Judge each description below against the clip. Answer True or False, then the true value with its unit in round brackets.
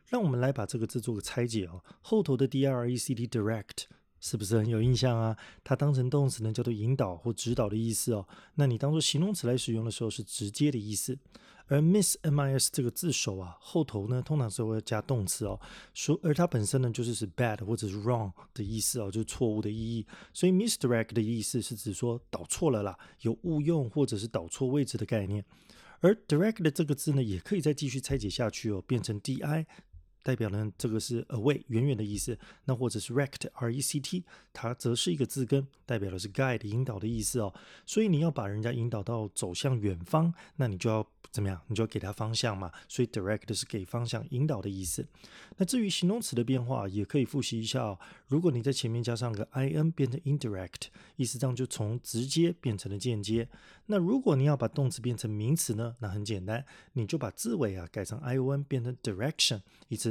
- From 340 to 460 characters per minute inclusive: True (370 characters per minute)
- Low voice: True (120 Hz)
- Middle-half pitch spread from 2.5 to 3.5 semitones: False (4.1 semitones)